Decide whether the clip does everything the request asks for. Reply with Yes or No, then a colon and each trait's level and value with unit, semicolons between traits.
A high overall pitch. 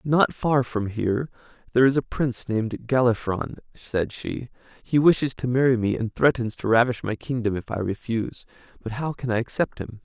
No: low, 120 Hz